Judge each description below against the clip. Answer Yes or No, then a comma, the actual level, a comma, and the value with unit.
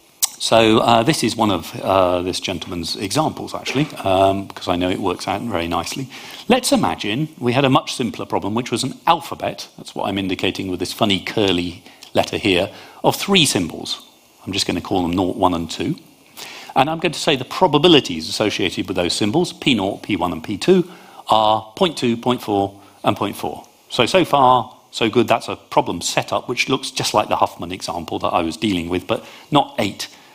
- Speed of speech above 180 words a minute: Yes, average, 195 wpm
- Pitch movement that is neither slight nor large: No, wide, 5.7 semitones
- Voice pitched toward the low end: Yes, low, 115 Hz